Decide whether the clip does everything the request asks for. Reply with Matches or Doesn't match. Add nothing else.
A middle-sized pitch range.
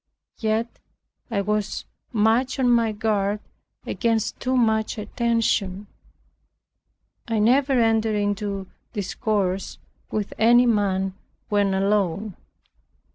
Doesn't match